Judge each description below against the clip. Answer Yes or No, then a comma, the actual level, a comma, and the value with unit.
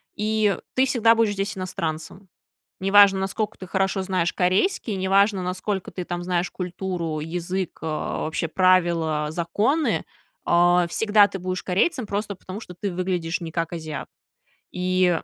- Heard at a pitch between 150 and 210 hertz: Yes, medium, 185 Hz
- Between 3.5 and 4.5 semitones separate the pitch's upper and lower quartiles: No, narrow, 2.6 semitones